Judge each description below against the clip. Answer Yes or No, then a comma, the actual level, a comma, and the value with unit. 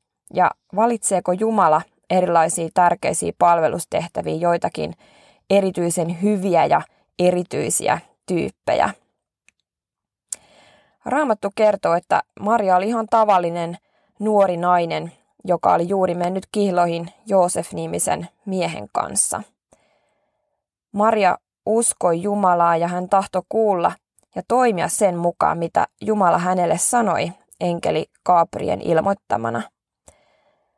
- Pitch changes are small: No, average, 3.2 semitones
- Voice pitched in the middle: Yes, medium, 180 Hz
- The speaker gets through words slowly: Yes, slow, 90 wpm